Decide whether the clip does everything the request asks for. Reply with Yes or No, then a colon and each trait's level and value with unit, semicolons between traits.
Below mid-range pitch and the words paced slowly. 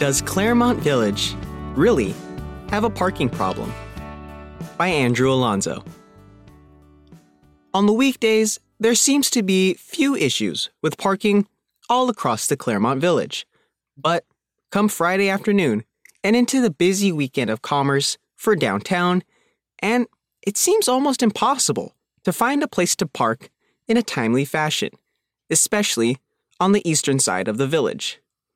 No: high, 190 Hz; slow, 130 wpm